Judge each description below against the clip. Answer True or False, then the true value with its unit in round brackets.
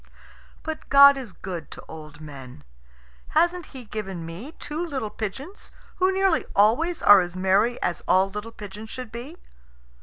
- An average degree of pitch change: False (7.9 semitones)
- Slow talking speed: False (155 wpm)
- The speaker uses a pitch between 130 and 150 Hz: False (220 Hz)